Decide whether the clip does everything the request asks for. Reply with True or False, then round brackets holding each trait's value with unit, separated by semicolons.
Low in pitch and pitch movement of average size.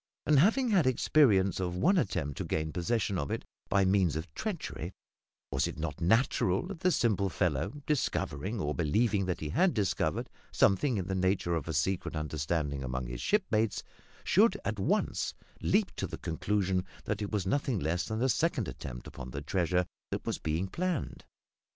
False (95 Hz; 6.7 semitones)